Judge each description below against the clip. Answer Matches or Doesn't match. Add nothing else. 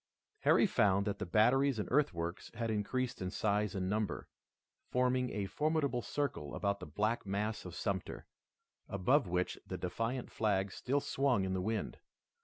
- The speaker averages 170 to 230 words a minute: Doesn't match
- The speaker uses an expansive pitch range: Doesn't match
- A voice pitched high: Doesn't match